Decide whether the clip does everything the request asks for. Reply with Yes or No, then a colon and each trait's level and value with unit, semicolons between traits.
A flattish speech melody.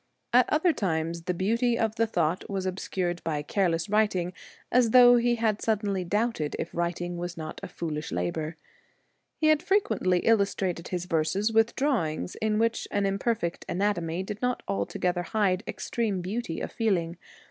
No: average, 4.7 semitones